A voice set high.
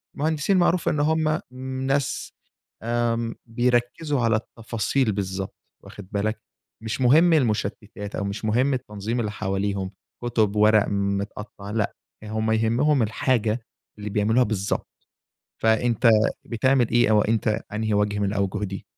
No: low, 110 Hz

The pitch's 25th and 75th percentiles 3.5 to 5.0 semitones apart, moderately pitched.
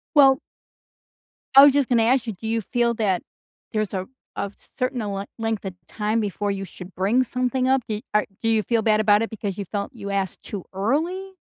No: average, 3.9 semitones; high, 220 Hz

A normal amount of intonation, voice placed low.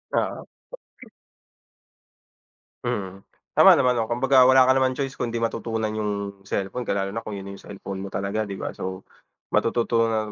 Yes: average, 3.5 semitones; low, 110 Hz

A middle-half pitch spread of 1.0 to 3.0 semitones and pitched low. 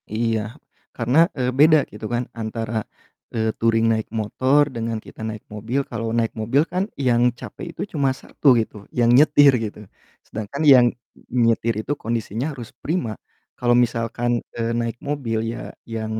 Yes: narrow, 2.6 semitones; low, 115 Hz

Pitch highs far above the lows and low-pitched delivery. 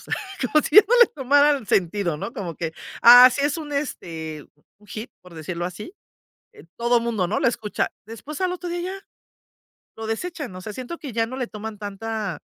No: wide, 6.3 semitones; high, 225 Hz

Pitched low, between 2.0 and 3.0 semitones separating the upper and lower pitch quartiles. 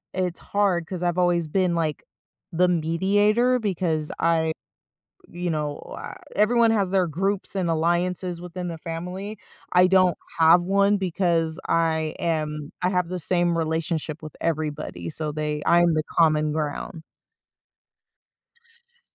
No: medium, 170 Hz; narrow, 2.6 semitones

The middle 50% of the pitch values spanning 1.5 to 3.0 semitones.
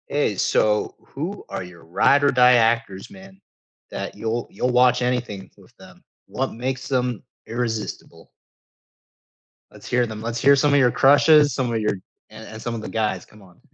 No: average, 3.4 semitones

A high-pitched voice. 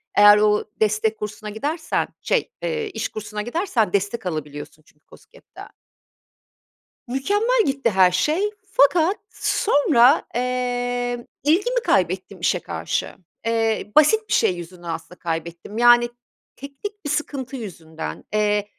Yes: high, 235 Hz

